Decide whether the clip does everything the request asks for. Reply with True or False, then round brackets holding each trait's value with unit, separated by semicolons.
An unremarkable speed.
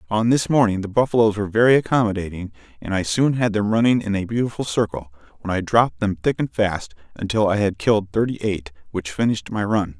False (210 wpm)